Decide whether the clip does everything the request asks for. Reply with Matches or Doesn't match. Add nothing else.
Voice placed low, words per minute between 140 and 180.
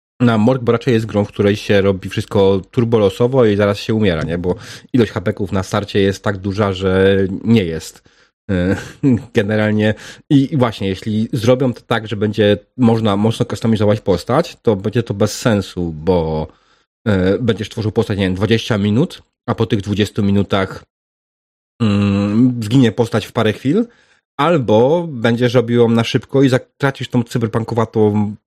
Matches